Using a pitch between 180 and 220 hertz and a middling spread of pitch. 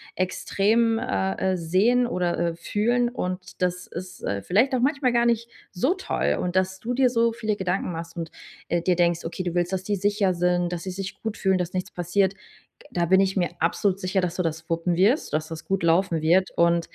Yes: medium, 185 Hz; average, 3.2 semitones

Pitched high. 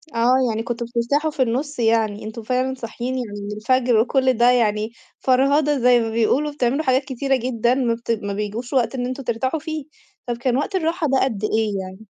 Yes: high, 245 Hz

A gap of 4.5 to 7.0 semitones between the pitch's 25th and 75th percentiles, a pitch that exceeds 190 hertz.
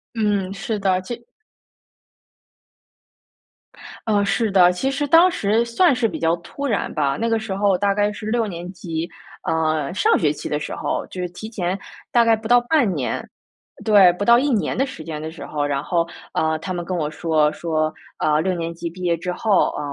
No: average, 5.2 semitones; medium, 185 Hz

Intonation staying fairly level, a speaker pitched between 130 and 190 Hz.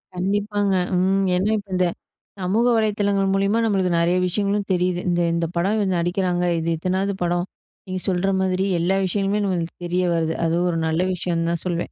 Yes: narrow, 2.2 semitones; medium, 185 Hz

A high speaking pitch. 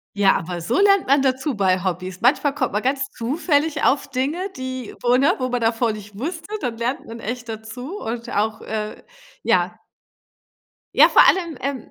Yes: very high, 250 Hz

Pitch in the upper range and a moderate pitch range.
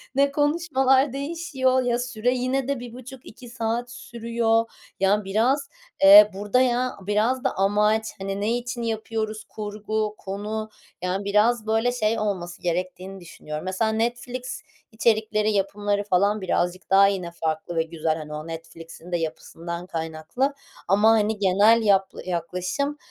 Yes: high, 215 Hz; average, 4.3 semitones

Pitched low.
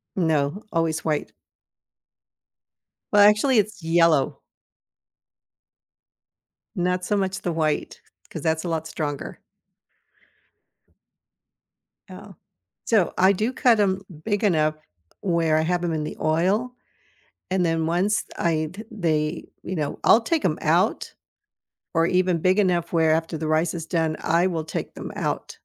No: medium, 170 Hz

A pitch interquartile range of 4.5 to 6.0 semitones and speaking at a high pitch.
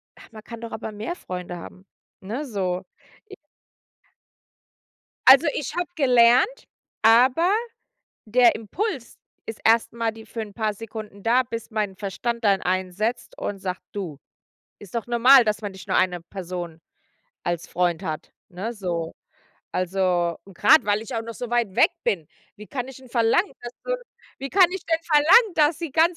Yes: average, 5.1 semitones; high, 225 Hz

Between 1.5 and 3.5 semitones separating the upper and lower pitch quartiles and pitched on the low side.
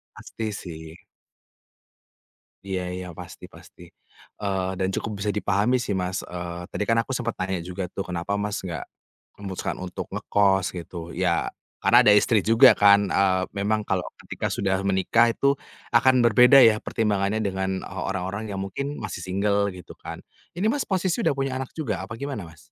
Yes: average, 3.2 semitones; low, 100 Hz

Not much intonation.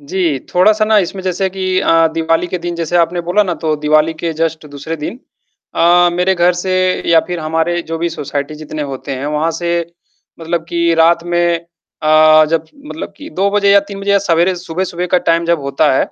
Yes: narrow, 2.2 semitones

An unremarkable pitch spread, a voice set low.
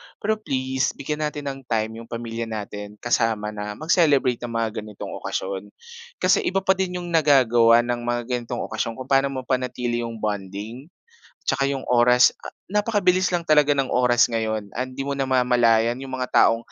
Yes: average, 3.4 semitones; low, 125 Hz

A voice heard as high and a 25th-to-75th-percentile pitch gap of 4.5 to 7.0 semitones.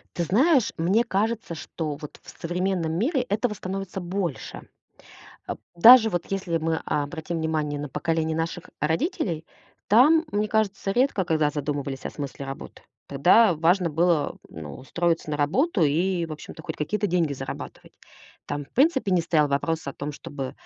No: medium, 170 Hz; average, 5.0 semitones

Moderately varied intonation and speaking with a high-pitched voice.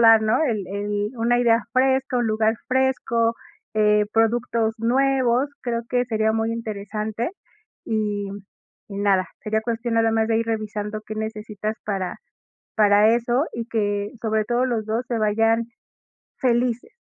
No: narrow, 1.9 semitones; high, 225 Hz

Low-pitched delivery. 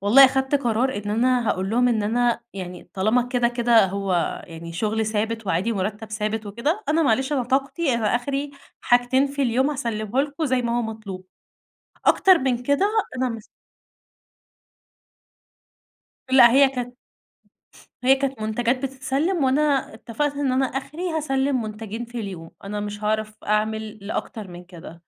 No: high, 240 Hz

